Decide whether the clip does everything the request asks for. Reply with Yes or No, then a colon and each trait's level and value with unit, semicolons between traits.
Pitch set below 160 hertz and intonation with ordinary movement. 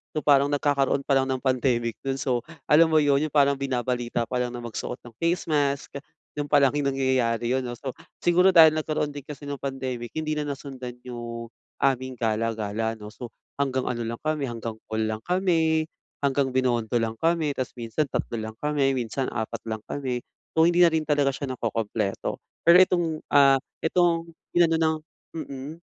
Yes: low, 135 Hz; average, 4.1 semitones